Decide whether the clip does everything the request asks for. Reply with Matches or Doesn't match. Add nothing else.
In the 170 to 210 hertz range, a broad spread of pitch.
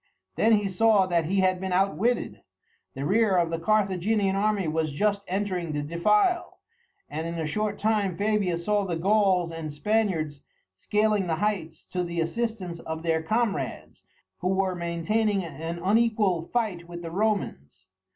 Doesn't match